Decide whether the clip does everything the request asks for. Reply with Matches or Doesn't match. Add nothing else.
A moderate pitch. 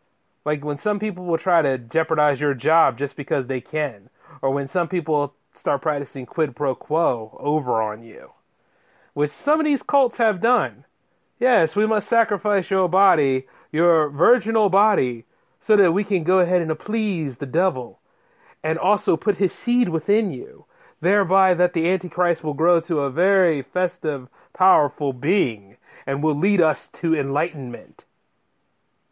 Matches